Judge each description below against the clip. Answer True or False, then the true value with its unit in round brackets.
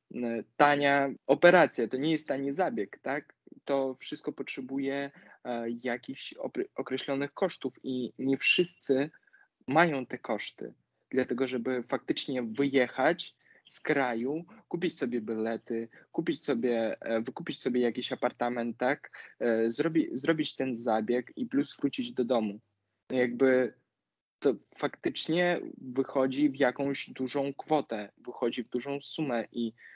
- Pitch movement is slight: False (3.1 semitones)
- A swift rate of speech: False (120 wpm)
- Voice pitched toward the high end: False (130 Hz)